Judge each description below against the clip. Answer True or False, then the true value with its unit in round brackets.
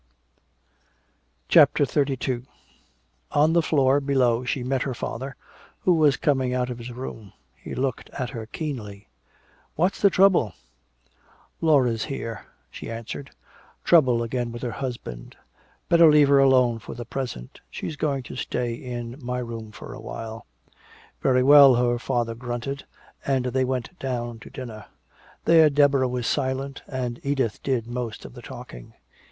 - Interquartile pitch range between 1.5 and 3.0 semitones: True (2.7 semitones)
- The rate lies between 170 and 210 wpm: False (150 wpm)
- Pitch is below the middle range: True (125 Hz)